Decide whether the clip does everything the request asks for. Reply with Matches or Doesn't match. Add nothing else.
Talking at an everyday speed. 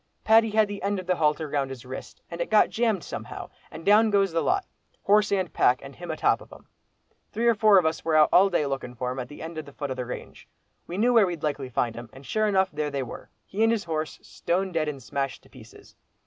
Doesn't match